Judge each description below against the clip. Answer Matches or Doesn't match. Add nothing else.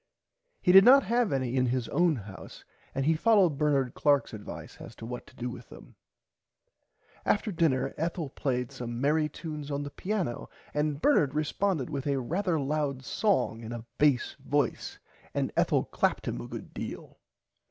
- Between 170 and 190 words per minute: Matches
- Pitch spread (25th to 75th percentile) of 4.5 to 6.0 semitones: Matches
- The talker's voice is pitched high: Doesn't match